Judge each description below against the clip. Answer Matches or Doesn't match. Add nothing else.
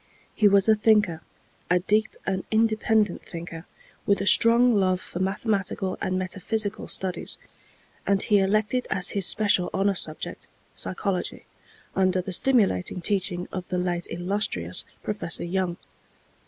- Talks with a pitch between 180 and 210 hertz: Matches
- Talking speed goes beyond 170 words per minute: Doesn't match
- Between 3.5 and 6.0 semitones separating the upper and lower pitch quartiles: Doesn't match